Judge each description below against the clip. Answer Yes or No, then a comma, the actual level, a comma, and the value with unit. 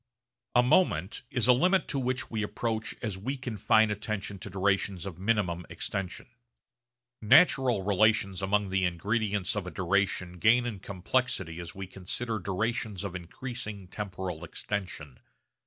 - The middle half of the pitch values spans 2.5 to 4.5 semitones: Yes, average, 3.3 semitones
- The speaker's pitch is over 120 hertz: No, low, 100 Hz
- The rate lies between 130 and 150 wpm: Yes, average, 140 wpm